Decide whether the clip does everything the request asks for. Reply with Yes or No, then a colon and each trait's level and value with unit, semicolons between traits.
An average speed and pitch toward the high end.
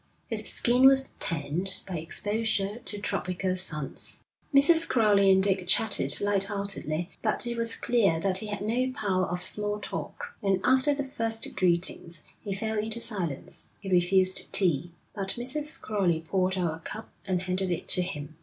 Yes: average, 170 wpm; high, 195 Hz